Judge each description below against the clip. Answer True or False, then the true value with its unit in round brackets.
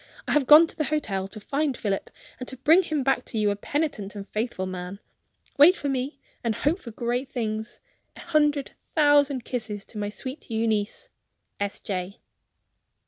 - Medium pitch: False (245 Hz)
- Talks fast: False (180 wpm)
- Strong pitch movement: True (5.8 semitones)